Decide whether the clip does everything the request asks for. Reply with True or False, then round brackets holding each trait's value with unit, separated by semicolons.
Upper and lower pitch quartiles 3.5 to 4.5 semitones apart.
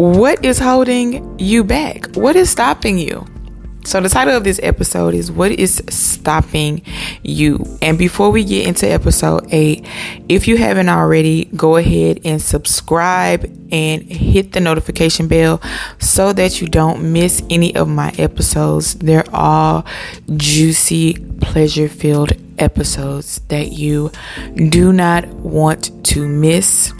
True (3.8 semitones)